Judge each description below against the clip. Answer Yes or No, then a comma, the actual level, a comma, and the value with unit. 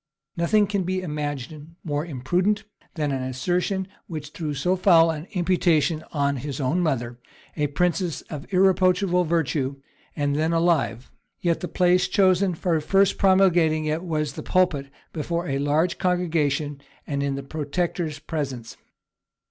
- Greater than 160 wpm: No, average, 145 wpm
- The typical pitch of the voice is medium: Yes, medium, 160 Hz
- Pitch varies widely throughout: No, average, 3.8 semitones